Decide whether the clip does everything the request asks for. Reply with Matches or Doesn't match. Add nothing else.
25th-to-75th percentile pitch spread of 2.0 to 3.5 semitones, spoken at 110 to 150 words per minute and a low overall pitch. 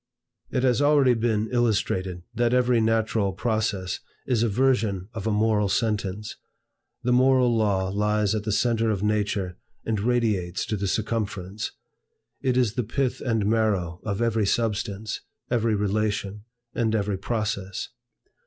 Matches